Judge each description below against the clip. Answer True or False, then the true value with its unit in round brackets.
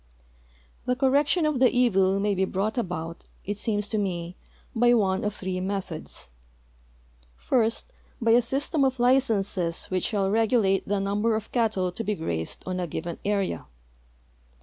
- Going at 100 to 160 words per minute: True (155 wpm)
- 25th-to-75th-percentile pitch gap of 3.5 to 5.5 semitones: True (4.1 semitones)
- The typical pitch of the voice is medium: False (205 Hz)